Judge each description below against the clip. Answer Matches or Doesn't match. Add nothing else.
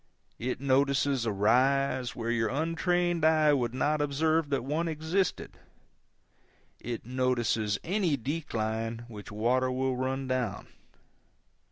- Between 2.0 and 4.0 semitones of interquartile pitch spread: Doesn't match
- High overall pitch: Doesn't match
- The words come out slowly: Matches